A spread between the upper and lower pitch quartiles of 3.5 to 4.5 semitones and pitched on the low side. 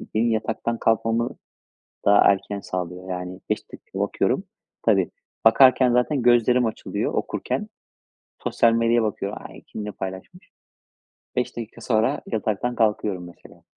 No: average, 3.1 semitones; low, 110 Hz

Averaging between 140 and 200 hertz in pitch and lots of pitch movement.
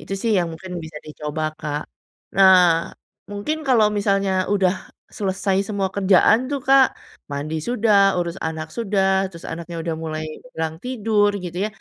No: high, 190 Hz; average, 3.9 semitones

